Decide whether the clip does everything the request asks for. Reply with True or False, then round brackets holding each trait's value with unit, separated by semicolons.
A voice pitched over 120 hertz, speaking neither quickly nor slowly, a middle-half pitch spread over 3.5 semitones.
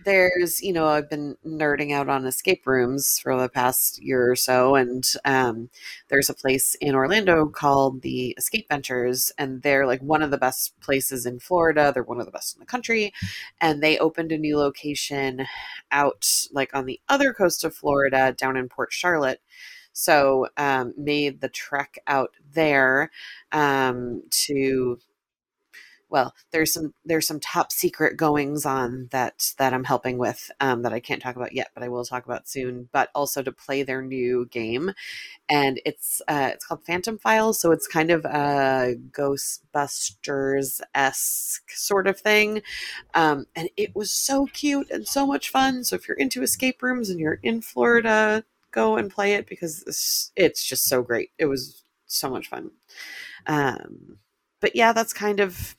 True (140 Hz; 175 wpm; 4.5 semitones)